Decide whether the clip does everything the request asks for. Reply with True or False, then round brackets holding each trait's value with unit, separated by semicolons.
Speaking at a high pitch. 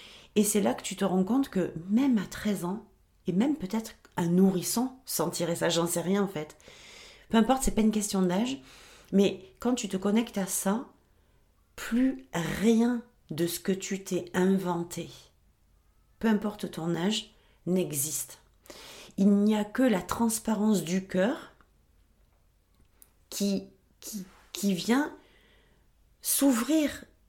True (195 Hz)